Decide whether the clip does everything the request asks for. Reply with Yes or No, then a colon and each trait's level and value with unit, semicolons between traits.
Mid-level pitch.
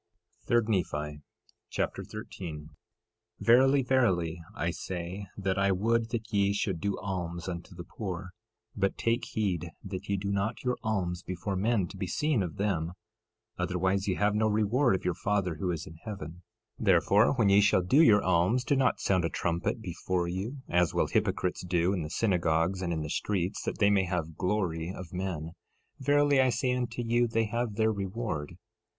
No: very low, 95 Hz